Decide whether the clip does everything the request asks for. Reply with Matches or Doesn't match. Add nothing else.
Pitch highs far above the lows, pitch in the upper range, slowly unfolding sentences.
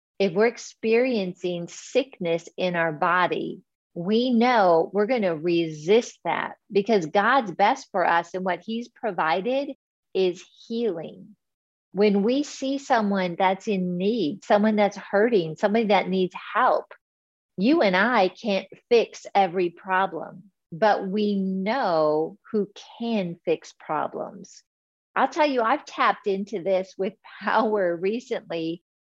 Doesn't match